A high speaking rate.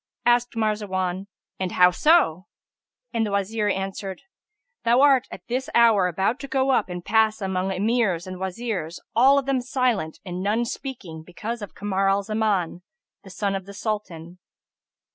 No: average, 160 wpm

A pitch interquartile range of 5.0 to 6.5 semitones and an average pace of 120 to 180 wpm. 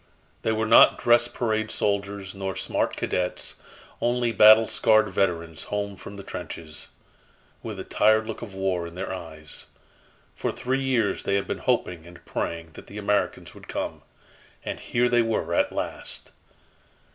No: average, 3.7 semitones; average, 160 wpm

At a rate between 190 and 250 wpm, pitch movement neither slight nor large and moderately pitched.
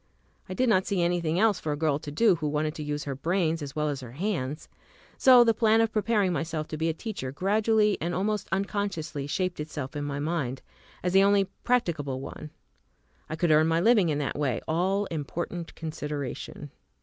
Yes: average, 200 wpm; average, 5.0 semitones; medium, 165 Hz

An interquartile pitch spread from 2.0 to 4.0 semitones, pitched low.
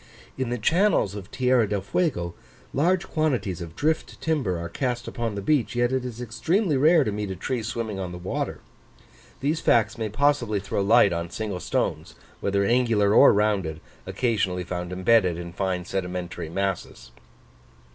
No: average, 5.3 semitones; low, 105 Hz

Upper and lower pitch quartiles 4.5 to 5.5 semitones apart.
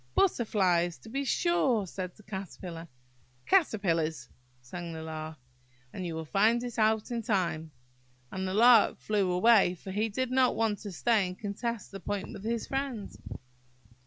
Yes: average, 4.8 semitones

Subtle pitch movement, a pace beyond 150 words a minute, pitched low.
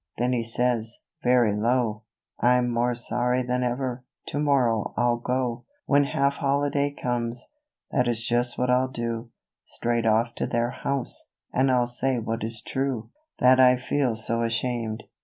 Yes: narrow, 1.6 semitones; average, 160 wpm; low, 120 Hz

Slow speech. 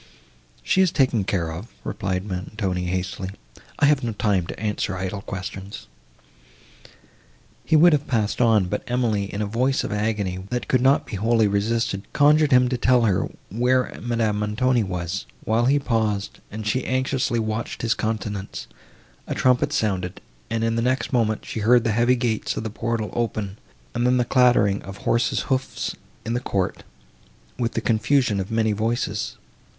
No: average, 170 wpm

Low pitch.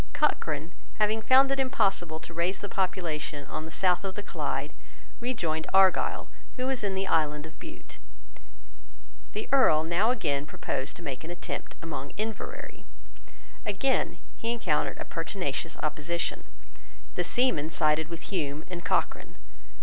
No: medium, 175 Hz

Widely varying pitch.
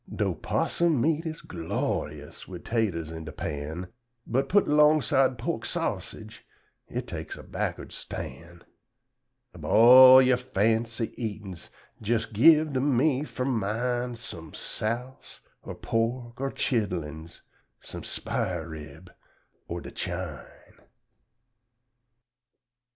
Yes: wide, 7.0 semitones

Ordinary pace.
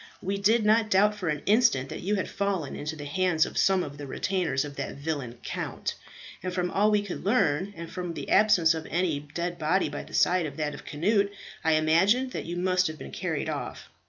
No: fast, 225 wpm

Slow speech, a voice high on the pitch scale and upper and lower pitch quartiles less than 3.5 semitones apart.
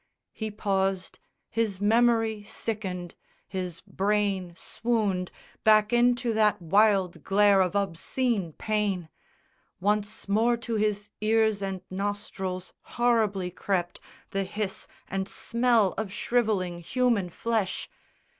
Yes: slow, 110 wpm; high, 205 Hz; average, 2.7 semitones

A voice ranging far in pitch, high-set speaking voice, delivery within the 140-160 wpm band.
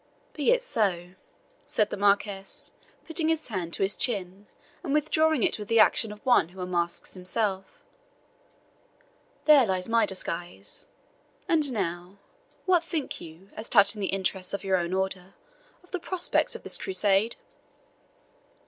Yes: wide, 6.5 semitones; high, 200 Hz; average, 150 wpm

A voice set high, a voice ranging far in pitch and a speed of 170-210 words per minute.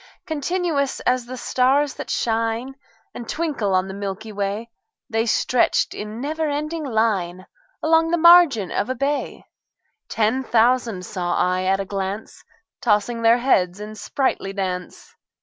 No: high, 230 Hz; wide, 5.8 semitones; average, 145 wpm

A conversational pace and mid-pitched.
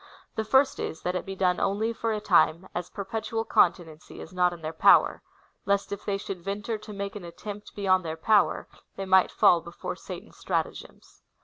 No: average, 190 wpm; high, 195 Hz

